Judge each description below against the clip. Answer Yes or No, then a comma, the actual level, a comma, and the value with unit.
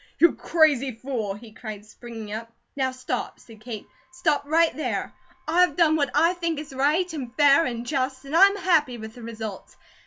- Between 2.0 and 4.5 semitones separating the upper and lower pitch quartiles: No, wide, 5.4 semitones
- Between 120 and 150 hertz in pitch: No, very high, 270 Hz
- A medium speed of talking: Yes, average, 185 wpm